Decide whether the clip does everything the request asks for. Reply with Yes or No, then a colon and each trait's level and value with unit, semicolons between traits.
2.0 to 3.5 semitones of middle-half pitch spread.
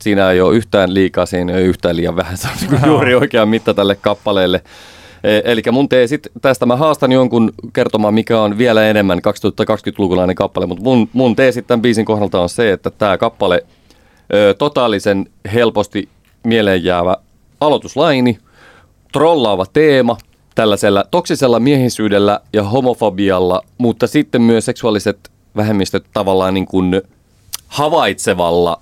No: average, 4.2 semitones